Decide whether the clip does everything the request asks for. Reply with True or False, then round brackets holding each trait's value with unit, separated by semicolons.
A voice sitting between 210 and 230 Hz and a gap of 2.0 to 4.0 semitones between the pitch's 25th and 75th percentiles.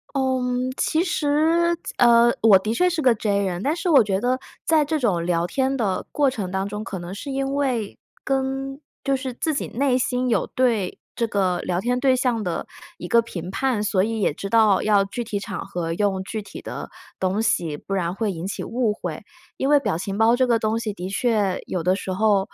False (220 Hz; 4.9 semitones)